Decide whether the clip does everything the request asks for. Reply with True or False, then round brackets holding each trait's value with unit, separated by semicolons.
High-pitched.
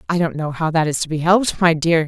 False (165 Hz)